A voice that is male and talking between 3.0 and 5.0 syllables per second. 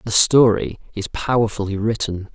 Yes: male; 4.9 syllables/s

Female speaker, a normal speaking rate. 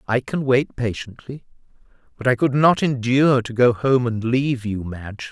No: male; average, 180 wpm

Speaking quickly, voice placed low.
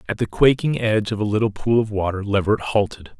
Yes: fast, 225 wpm; low, 105 Hz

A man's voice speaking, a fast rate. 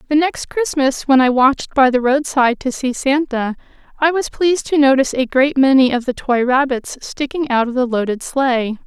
No: female; fast, 210 wpm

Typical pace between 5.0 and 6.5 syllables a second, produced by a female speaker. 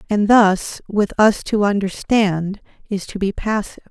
No: 4.3 syllables/s; female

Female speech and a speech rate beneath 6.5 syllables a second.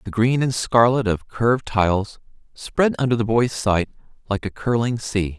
No: male; 4.7 syllables/s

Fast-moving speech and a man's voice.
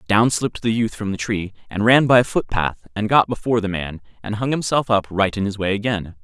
Yes: fast, 250 wpm; male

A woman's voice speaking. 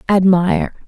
Yes: female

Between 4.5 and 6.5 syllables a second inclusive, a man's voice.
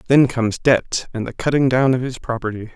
Yes: 5.6 syllables/s; male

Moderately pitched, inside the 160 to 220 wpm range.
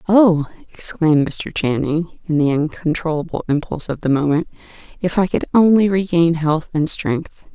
No: medium, 165 Hz; average, 150 wpm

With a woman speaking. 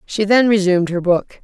Yes: female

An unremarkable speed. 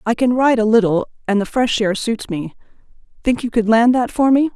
No: fast, 235 wpm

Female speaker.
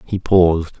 No: male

